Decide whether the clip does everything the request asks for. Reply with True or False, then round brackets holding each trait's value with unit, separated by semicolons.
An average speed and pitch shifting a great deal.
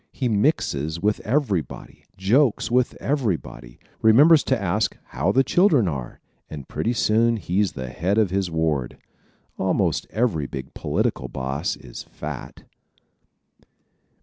False (125 wpm; 7.3 semitones)